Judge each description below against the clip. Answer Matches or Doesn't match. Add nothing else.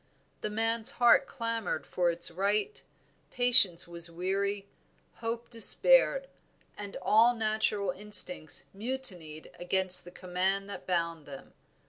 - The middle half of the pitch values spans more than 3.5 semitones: Matches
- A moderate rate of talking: Doesn't match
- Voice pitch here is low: Doesn't match